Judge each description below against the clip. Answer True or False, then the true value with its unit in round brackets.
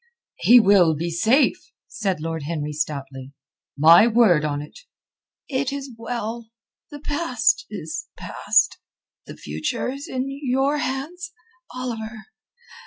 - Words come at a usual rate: False (115 wpm)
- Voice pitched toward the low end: False (225 Hz)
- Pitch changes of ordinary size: False (8.7 semitones)